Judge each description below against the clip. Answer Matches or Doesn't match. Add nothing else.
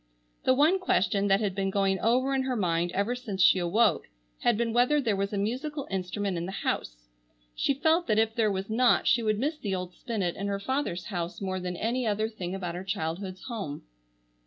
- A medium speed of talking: Doesn't match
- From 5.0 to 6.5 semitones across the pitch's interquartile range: Doesn't match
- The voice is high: Matches